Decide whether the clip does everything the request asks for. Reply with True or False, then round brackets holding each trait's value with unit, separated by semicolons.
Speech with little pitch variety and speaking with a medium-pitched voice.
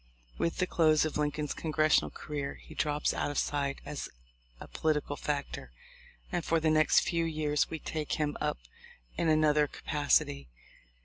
True (1.3 semitones; 150 Hz)